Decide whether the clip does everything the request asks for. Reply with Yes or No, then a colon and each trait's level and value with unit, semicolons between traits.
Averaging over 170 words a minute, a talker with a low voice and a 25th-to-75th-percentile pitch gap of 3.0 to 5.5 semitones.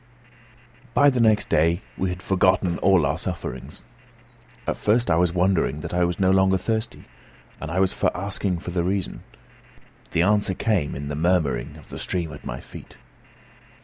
No: average, 180 wpm; very low, 90 Hz; narrow, 2.6 semitones